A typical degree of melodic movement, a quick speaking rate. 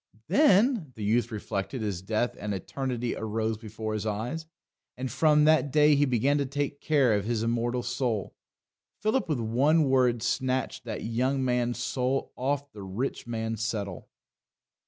No: average, 4.2 semitones; average, 155 wpm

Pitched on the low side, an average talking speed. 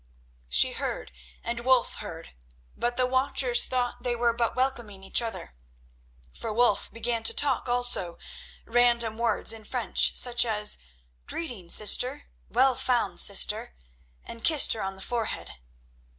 No: high, 235 Hz; average, 145 wpm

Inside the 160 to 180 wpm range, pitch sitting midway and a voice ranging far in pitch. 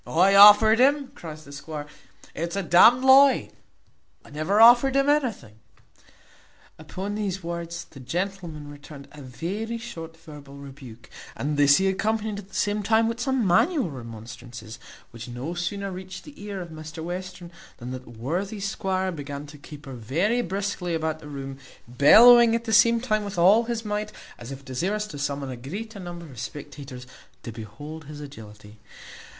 Yes: average, 170 wpm; medium, 170 Hz; wide, 6.8 semitones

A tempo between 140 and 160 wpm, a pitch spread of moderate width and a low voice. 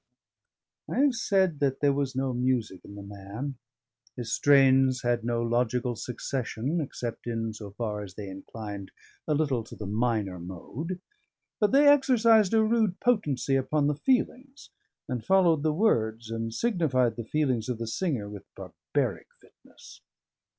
No: average, 150 wpm; wide, 6.2 semitones; low, 130 Hz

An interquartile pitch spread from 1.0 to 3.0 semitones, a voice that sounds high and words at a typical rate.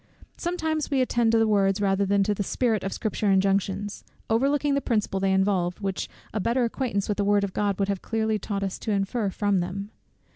No: narrow, 2.6 semitones; high, 205 Hz; fast, 215 wpm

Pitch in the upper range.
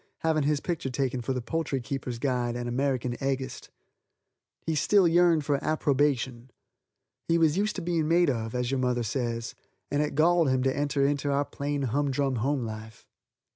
No: medium, 140 Hz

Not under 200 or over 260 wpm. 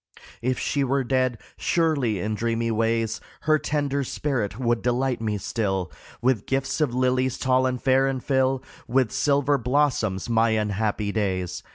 No: average, 155 wpm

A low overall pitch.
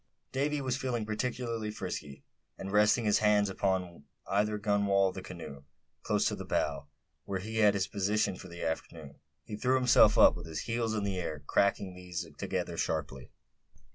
Yes: low, 100 Hz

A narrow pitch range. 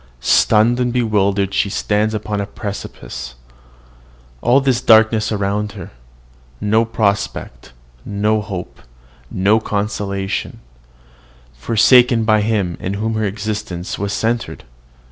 Yes: narrow, 1.9 semitones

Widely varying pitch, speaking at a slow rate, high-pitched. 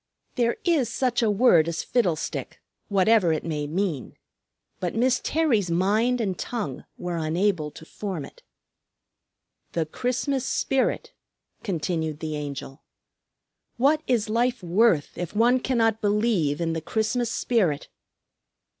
Yes: wide, 6.6 semitones; slow, 130 wpm; high, 205 Hz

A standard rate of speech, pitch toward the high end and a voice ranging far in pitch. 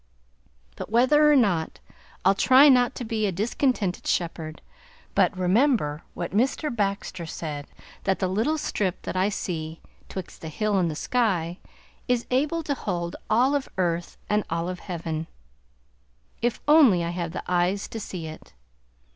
Yes: average, 160 wpm; high, 195 Hz; wide, 6.1 semitones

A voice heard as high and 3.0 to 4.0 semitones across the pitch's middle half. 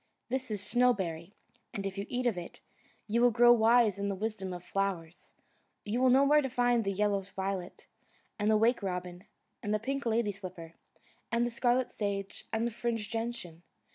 Yes: high, 215 Hz; average, 3.6 semitones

